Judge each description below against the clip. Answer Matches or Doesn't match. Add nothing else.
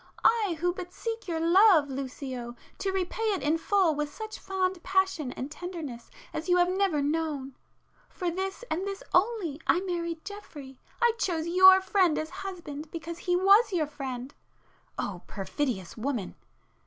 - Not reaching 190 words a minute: Matches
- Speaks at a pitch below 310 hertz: Doesn't match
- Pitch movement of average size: Matches